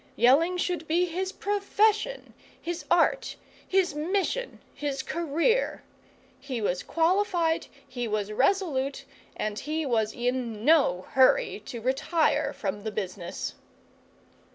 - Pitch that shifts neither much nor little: No, wide, 7.1 semitones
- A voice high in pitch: Yes, very high, 305 Hz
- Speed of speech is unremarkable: No, slow, 115 wpm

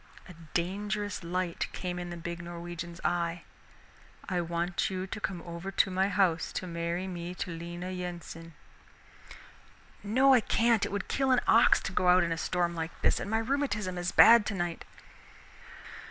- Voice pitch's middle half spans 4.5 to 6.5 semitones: No, narrow, 2.6 semitones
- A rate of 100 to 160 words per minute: No, average, 170 wpm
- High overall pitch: No, medium, 180 Hz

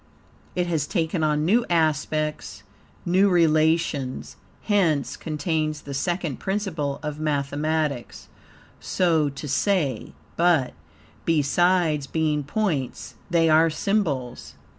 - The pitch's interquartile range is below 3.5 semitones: Yes, average, 3.1 semitones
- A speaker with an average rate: No, slow, 100 wpm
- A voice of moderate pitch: Yes, medium, 155 Hz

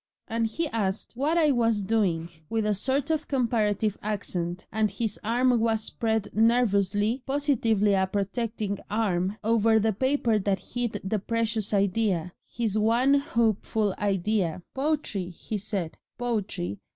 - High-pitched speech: Yes, high, 220 Hz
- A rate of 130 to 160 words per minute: Yes, average, 140 wpm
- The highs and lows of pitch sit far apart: No, average, 2.9 semitones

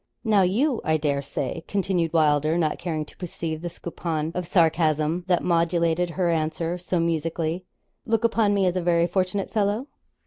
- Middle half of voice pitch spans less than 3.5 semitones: Yes, narrow, 2.6 semitones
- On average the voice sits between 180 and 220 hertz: No, medium, 170 Hz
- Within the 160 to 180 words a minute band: Yes, average, 170 wpm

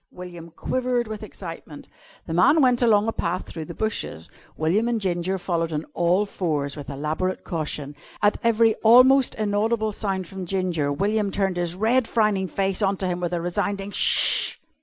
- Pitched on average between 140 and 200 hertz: Yes, high, 190 Hz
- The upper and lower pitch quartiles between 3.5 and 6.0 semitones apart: Yes, average, 4.3 semitones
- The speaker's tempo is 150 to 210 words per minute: Yes, average, 175 wpm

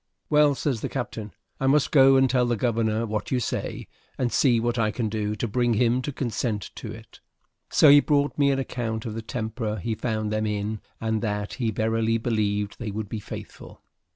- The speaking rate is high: Yes, fast, 210 wpm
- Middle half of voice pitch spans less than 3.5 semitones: Yes, average, 2.9 semitones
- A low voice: Yes, low, 115 Hz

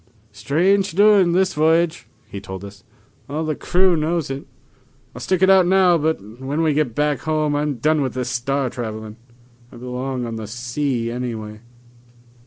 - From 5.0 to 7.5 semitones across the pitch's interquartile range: Yes, wide, 5.4 semitones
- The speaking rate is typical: Yes, average, 170 wpm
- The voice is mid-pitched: Yes, medium, 145 Hz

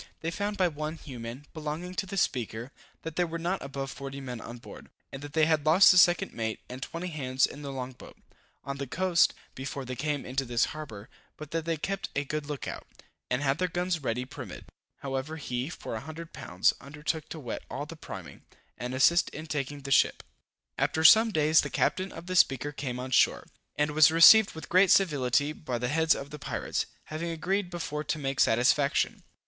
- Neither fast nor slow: No, fast, 210 wpm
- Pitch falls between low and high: Yes, medium, 150 Hz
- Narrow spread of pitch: No, average, 3.9 semitones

